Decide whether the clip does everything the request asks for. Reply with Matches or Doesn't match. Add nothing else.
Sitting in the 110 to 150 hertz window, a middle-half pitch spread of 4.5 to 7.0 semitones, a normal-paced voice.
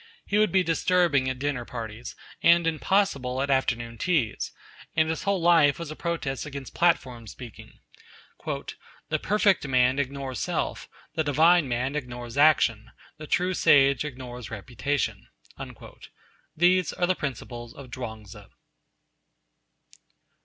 Doesn't match